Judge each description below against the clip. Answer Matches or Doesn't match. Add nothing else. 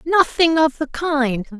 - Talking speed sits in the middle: Matches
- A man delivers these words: Doesn't match